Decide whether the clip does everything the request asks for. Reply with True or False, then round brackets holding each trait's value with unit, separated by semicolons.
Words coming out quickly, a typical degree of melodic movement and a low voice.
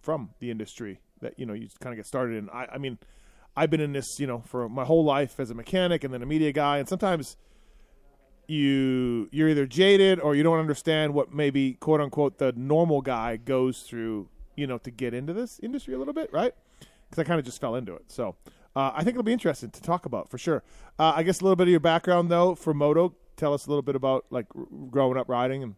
False (250 wpm; 4.5 semitones; 145 Hz)